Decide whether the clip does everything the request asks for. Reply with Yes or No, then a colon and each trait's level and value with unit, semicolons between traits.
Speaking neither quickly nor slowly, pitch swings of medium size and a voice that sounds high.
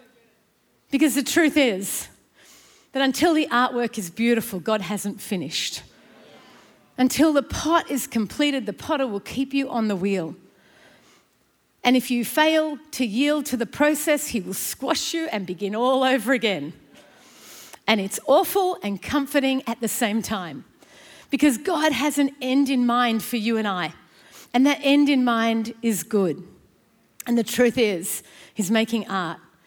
Yes: average, 160 wpm; average, 4.5 semitones; high, 245 Hz